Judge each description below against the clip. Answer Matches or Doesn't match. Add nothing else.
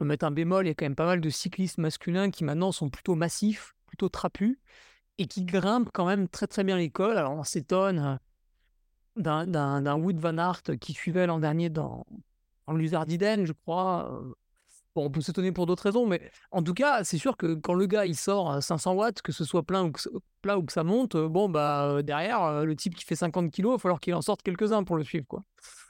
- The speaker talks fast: Matches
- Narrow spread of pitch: Doesn't match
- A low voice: Doesn't match